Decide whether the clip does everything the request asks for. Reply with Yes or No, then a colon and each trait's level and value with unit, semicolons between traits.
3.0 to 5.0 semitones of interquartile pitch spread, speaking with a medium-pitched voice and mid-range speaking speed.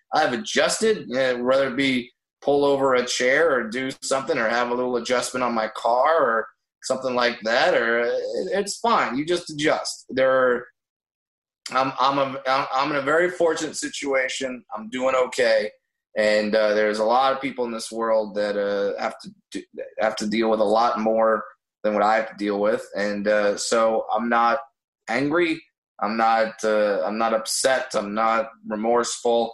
No: average, 3.9 semitones; low, 125 Hz; average, 180 wpm